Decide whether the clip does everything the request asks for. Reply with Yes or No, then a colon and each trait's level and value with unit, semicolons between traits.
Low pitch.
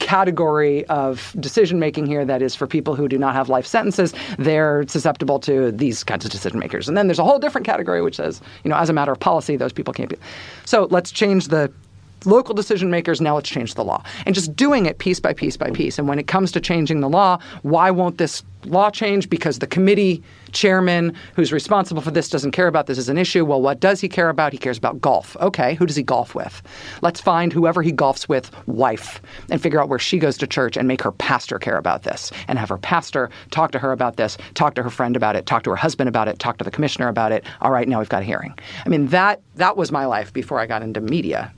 No: medium, 155 Hz